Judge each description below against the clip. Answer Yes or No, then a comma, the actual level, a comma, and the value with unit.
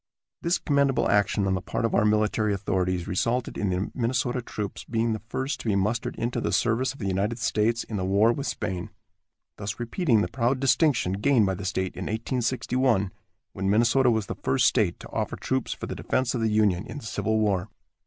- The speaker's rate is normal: No, fast, 210 wpm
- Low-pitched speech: Yes, low, 110 Hz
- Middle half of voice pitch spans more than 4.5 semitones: No, average, 3.8 semitones